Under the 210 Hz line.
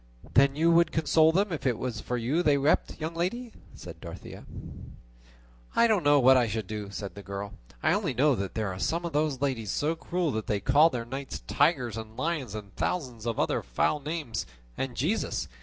Yes: medium, 140 Hz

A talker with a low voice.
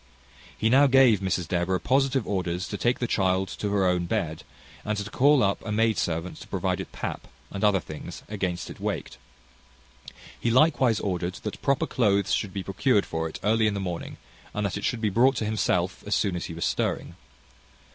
Yes: low, 100 Hz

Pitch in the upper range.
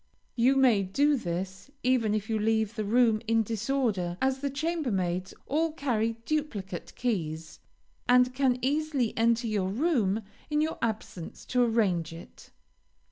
Yes: high, 230 Hz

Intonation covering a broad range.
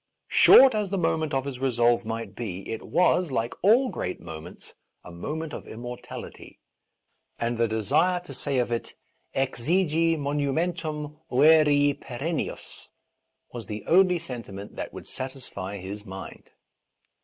Yes: wide, 6.0 semitones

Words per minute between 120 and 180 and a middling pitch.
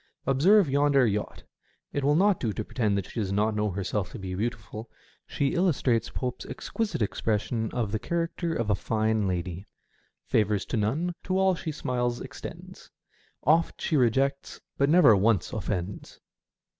No: average, 170 wpm; low, 115 Hz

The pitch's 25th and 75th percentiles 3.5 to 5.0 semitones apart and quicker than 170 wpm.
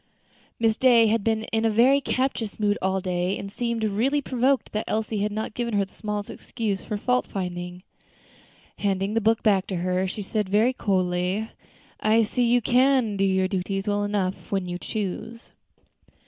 No: average, 3.1 semitones; average, 180 wpm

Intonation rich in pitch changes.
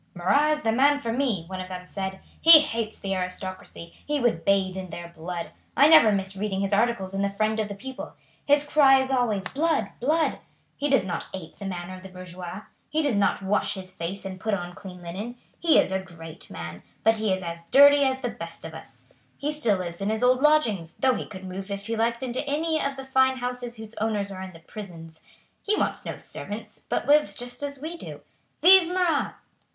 Yes: wide, 6.2 semitones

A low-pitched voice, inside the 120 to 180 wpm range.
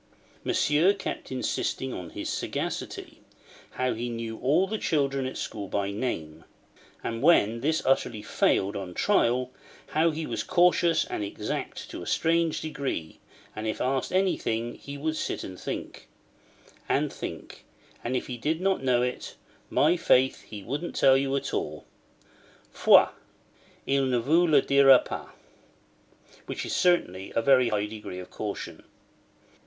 Yes: low, 130 Hz; average, 150 wpm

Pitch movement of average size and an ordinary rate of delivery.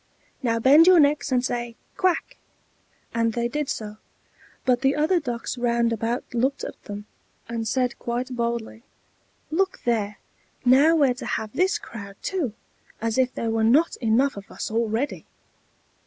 Yes: average, 3.6 semitones; average, 155 wpm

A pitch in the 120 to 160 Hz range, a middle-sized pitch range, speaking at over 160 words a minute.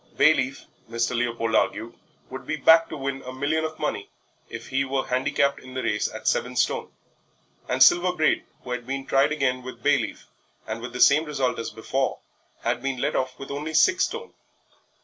Yes: low, 135 Hz; average, 3.1 semitones; average, 190 wpm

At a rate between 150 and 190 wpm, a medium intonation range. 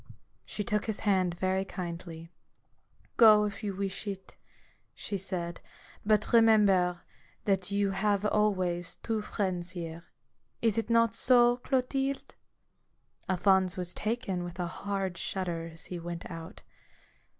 No: average, 140 wpm; average, 3.1 semitones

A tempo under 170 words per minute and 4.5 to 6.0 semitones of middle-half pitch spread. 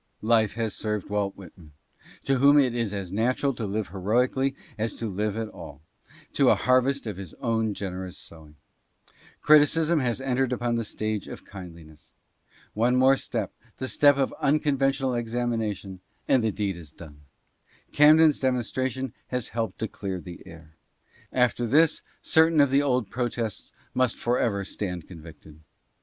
Yes: average, 160 wpm; average, 5.0 semitones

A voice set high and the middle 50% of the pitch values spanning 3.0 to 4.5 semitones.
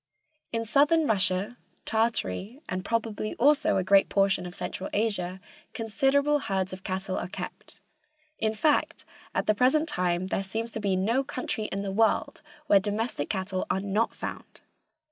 Yes: high, 210 Hz; average, 3.4 semitones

